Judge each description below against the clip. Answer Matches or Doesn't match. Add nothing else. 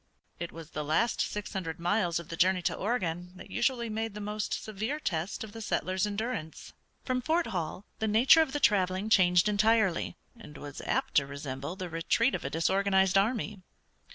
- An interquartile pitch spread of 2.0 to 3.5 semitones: Doesn't match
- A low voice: Doesn't match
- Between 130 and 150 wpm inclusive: Doesn't match